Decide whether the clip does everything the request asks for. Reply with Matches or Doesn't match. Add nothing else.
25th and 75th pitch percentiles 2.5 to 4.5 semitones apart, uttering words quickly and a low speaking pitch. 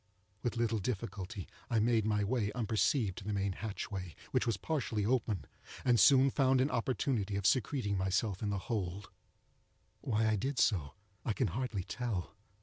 Doesn't match